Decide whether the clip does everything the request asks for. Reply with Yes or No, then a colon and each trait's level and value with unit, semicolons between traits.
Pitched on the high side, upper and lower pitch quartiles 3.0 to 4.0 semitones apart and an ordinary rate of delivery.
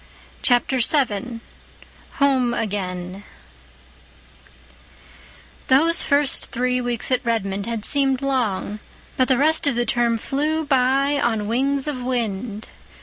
No: very high, 250 Hz; average, 3.4 semitones; slow, 115 wpm